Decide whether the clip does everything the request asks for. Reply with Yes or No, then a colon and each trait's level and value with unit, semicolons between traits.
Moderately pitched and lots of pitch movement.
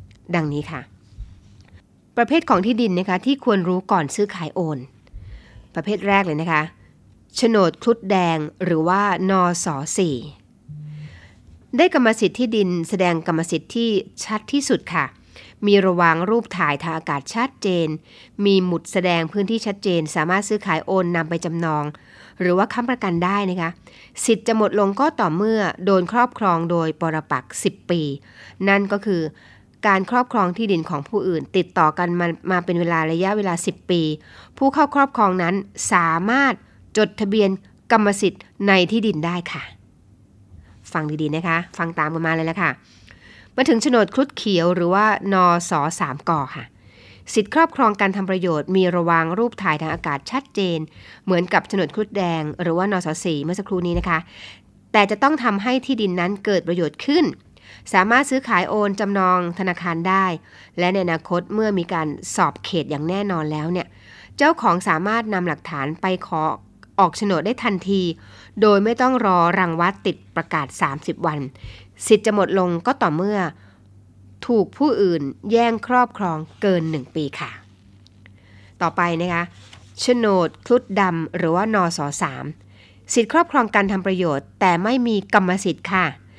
No: medium, 180 Hz; average, 4.6 semitones